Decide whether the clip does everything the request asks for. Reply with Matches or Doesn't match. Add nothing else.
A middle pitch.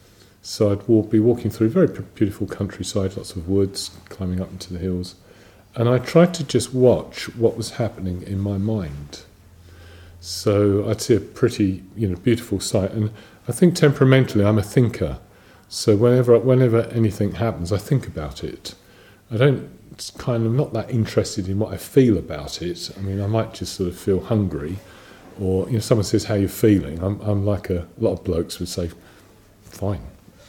Doesn't match